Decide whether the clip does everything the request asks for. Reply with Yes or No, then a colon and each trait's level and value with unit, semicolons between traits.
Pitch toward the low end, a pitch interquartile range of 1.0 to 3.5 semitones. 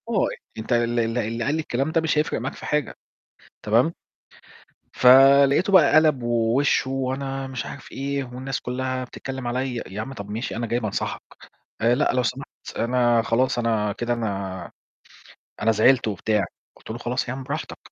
Yes: low, 125 Hz; average, 2.9 semitones